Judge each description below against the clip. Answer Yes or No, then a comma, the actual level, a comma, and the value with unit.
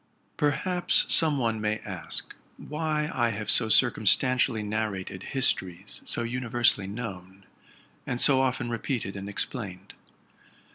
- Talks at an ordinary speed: No, slow, 130 wpm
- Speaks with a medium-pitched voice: No, low, 115 Hz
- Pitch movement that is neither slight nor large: Yes, average, 4.3 semitones